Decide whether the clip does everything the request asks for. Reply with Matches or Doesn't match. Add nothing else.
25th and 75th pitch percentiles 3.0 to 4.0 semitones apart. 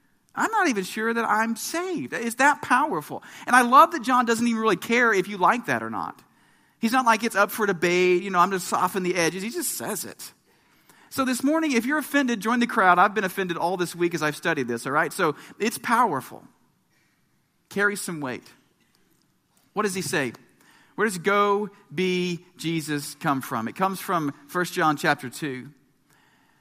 Doesn't match